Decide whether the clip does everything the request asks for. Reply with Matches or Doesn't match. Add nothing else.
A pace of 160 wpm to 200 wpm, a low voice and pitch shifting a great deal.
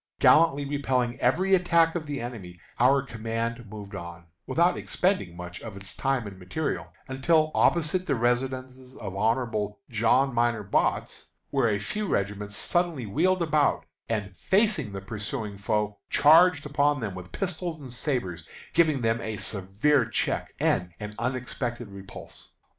Doesn't match